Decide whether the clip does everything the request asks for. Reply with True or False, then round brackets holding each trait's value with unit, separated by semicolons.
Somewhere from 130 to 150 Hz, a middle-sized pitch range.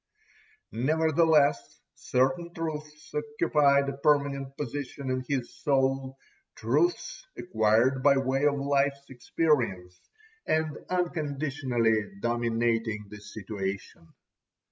True (140 Hz; 4.1 semitones)